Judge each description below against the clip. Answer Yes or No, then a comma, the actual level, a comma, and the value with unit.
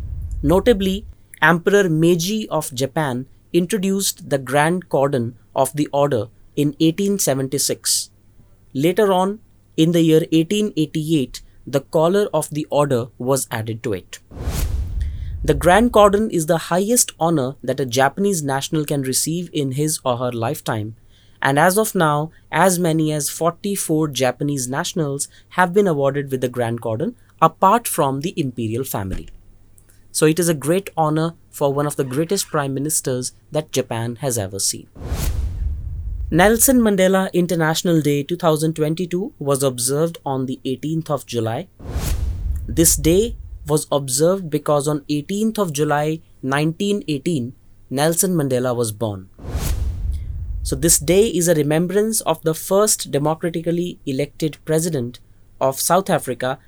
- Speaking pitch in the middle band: Yes, medium, 145 Hz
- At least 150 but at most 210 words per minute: No, slow, 135 wpm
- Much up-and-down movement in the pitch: Yes, wide, 6.0 semitones